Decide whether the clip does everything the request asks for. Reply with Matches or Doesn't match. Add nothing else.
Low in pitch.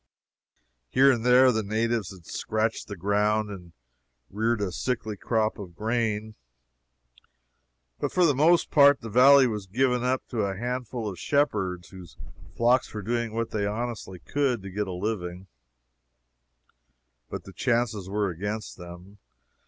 Matches